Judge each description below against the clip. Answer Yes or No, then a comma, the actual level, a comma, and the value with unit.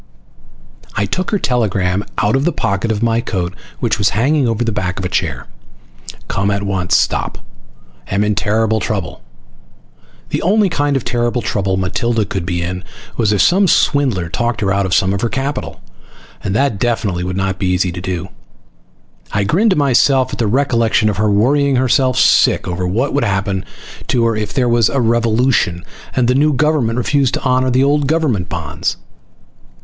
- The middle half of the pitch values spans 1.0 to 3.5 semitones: No, average, 5.1 semitones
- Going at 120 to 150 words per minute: No, average, 190 wpm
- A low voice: Yes, low, 110 Hz